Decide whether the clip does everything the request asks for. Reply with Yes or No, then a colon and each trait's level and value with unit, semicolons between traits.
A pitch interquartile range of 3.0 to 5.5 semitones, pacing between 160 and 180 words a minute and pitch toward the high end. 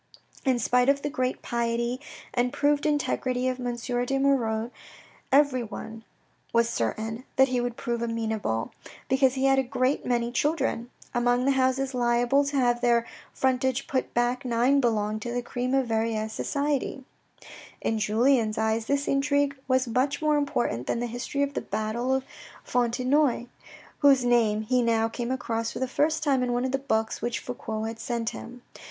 No: narrow, 2.6 semitones; average, 170 wpm; high, 245 Hz